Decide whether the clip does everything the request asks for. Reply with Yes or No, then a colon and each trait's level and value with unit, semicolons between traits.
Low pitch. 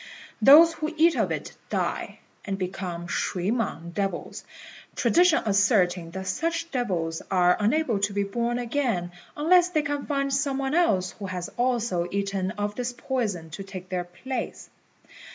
No: high, 205 Hz